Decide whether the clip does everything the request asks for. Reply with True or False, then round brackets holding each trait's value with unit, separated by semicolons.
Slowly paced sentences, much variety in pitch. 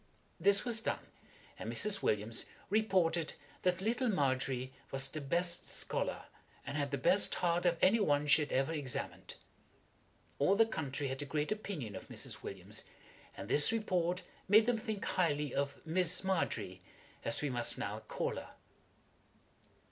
False (155 wpm; 5.9 semitones)